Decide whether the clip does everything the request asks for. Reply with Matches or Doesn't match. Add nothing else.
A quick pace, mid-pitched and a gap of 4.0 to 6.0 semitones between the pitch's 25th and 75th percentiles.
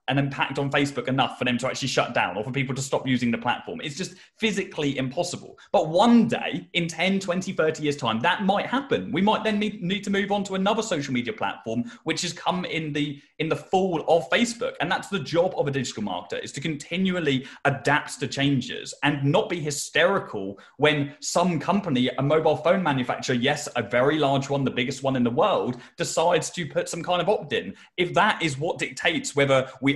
Matches